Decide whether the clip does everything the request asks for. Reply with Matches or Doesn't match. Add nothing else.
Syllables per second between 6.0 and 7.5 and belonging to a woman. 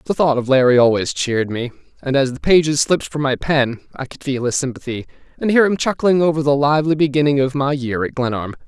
Doesn't match